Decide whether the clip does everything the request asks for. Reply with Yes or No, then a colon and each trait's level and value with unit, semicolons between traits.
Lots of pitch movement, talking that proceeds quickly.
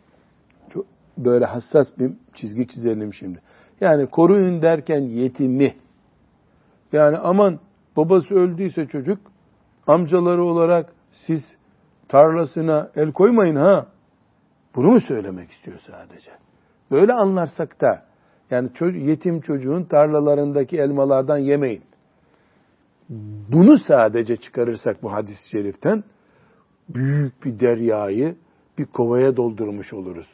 No: wide, 5.9 semitones; slow, 95 wpm